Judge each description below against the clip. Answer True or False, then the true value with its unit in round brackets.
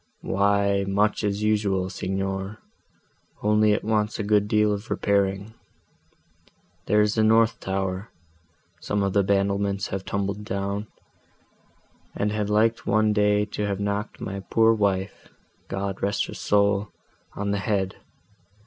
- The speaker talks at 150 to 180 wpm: False (135 wpm)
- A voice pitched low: True (100 Hz)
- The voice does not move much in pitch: True (1.3 semitones)